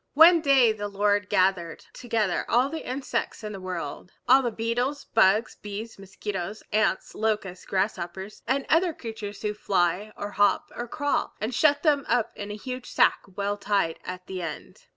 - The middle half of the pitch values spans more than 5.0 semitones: No, average, 4.1 semitones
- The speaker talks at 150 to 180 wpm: Yes, average, 170 wpm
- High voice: Yes, high, 210 Hz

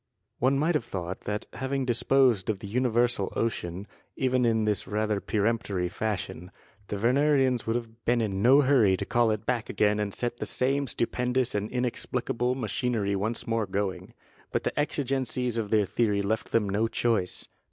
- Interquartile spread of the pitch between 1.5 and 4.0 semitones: Yes, average, 3.4 semitones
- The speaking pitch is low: Yes, low, 115 Hz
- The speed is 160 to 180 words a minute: Yes, average, 175 wpm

